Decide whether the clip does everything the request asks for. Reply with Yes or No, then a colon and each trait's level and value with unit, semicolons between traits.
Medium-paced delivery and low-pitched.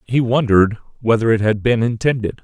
Yes: average, 175 wpm; low, 115 Hz